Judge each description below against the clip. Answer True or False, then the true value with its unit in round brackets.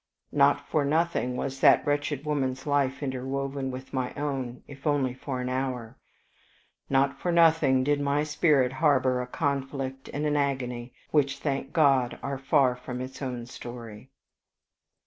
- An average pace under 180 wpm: True (150 wpm)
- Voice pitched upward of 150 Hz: False (135 Hz)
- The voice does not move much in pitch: True (2.0 semitones)